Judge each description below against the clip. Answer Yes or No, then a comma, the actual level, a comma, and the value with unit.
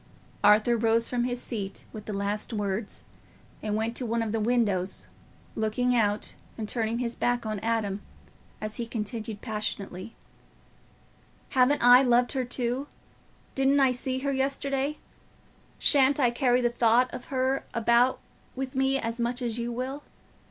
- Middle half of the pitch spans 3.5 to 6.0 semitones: No, average, 2.8 semitones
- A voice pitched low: No, high, 235 Hz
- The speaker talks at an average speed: Yes, average, 155 wpm